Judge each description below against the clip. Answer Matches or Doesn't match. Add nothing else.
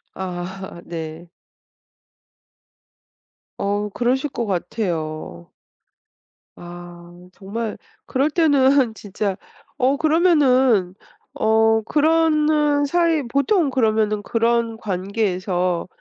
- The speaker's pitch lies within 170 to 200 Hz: Doesn't match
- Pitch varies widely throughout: Matches